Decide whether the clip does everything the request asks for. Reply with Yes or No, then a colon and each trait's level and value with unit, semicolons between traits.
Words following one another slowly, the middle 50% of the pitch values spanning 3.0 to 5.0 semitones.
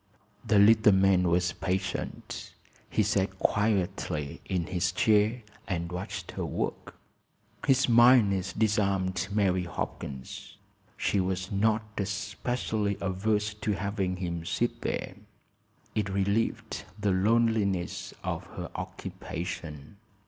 No: slow, 110 wpm; narrow, 2.6 semitones